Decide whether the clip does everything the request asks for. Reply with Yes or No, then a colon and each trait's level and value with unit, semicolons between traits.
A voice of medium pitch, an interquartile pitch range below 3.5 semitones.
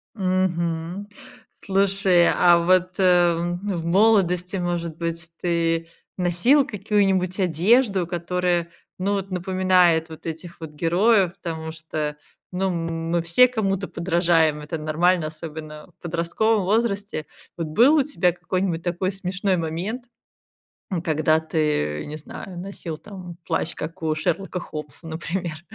Yes: medium, 175 Hz; average, 2.7 semitones